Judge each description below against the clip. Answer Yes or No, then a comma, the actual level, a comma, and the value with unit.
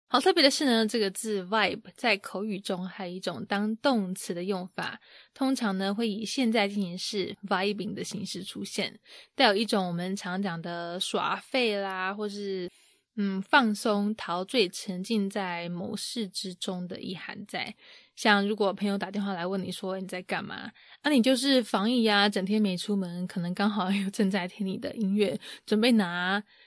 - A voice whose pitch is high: Yes, high, 200 Hz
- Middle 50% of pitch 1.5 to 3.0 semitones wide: Yes, narrow, 2.6 semitones